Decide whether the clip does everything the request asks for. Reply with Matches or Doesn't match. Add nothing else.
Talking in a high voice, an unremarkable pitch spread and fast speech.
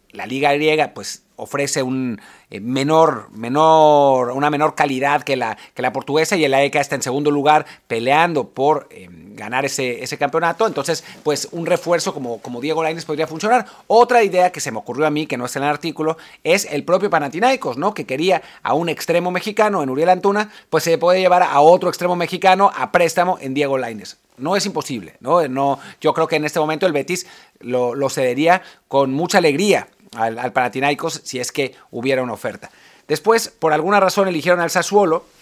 Doesn't match